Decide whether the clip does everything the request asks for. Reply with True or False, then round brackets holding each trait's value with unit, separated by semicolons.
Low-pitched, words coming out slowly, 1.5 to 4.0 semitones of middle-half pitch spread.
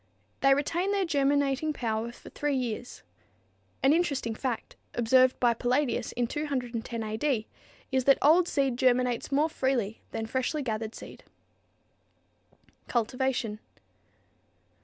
False (255 Hz; 120 wpm; 3.3 semitones)